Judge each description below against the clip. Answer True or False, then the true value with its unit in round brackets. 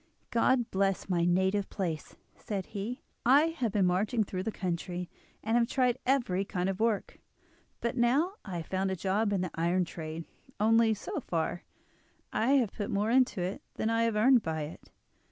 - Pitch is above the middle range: True (200 Hz)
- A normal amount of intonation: True (4.3 semitones)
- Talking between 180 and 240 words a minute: True (185 wpm)